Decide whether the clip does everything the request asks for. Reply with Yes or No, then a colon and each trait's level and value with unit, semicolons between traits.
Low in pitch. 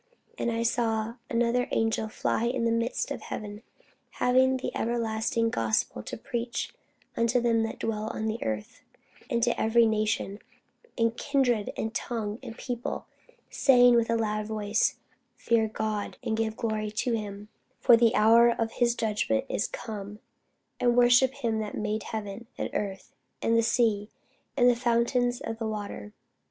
No: high, 225 Hz